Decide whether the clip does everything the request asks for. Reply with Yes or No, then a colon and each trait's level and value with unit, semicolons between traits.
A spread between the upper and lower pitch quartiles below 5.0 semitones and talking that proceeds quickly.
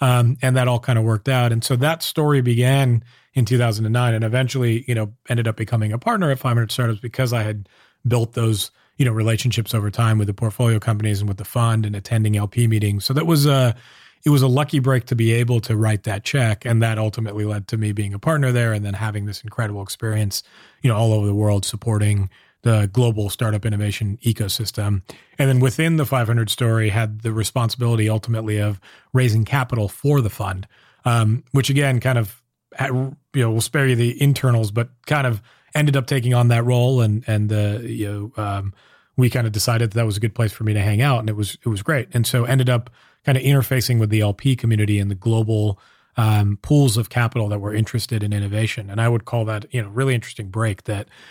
Yes: average, 2.8 semitones; fast, 225 wpm